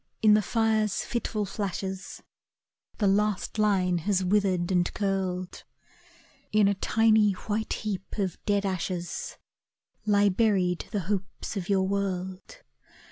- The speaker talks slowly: Yes, slow, 125 wpm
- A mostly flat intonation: Yes, narrow, 2.2 semitones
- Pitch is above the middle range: Yes, high, 200 Hz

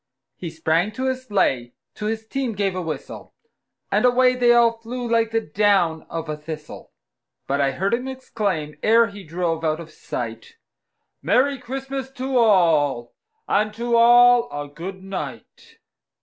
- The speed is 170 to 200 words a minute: No, average, 160 wpm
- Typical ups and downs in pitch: No, wide, 7.1 semitones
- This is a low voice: No, high, 210 Hz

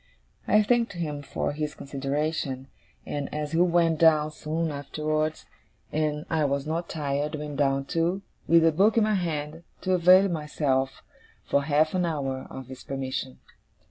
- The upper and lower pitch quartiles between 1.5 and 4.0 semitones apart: Yes, average, 2.8 semitones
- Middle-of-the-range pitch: Yes, medium, 155 Hz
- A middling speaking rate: Yes, average, 160 wpm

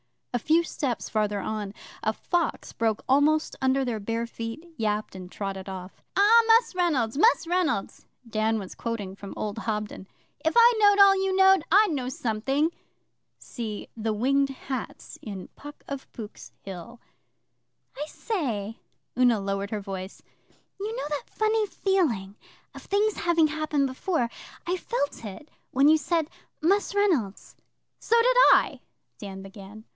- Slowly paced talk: No, average, 150 wpm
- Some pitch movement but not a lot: No, wide, 8.4 semitones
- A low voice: No, very high, 260 Hz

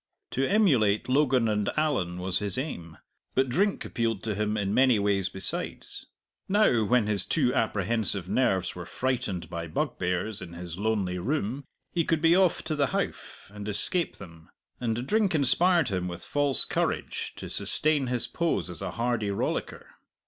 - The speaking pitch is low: Yes, low, 115 Hz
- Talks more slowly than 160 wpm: No, average, 165 wpm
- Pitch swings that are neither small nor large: No, wide, 6.4 semitones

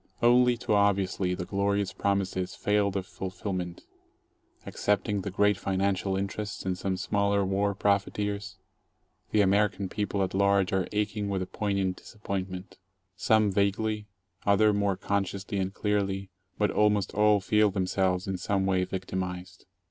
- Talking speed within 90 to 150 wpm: Yes, average, 145 wpm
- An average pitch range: No, narrow, 1.5 semitones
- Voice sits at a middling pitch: No, low, 100 Hz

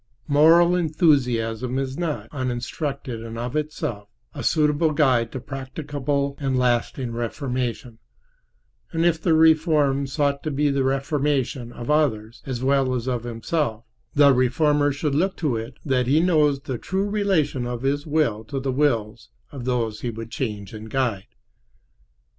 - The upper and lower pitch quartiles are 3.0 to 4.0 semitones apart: Yes, average, 3.7 semitones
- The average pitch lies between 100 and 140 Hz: Yes, low, 135 Hz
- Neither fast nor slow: Yes, average, 150 wpm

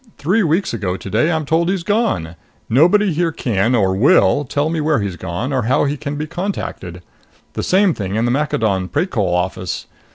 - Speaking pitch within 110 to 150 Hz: Yes, medium, 140 Hz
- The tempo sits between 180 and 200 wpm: Yes, average, 190 wpm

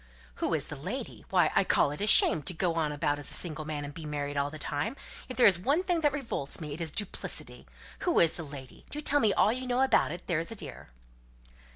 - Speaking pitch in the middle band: Yes, medium, 165 Hz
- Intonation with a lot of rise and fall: Yes, wide, 8.6 semitones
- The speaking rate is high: Yes, fast, 250 wpm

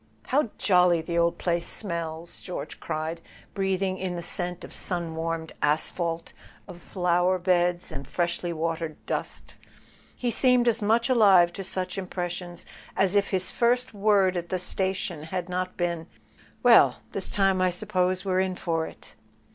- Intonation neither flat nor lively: No, narrow, 2.0 semitones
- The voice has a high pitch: No, medium, 180 Hz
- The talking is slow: No, average, 160 wpm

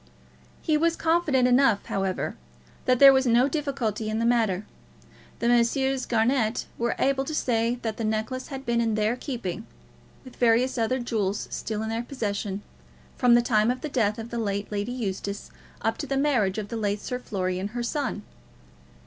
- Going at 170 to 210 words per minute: Yes, average, 185 wpm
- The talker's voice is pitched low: No, high, 235 Hz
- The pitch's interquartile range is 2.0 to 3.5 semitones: Yes, average, 3.2 semitones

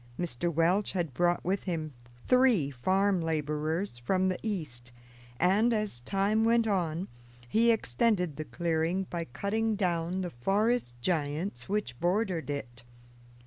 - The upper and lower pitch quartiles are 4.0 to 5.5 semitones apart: Yes, average, 4.7 semitones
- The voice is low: No, medium, 175 Hz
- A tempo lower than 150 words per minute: Yes, slow, 135 wpm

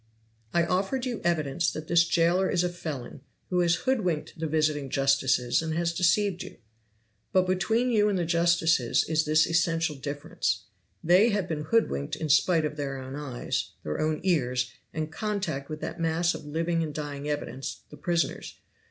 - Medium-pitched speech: Yes, medium, 160 Hz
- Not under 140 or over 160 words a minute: No, average, 175 wpm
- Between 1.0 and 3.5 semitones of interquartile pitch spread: Yes, average, 3.1 semitones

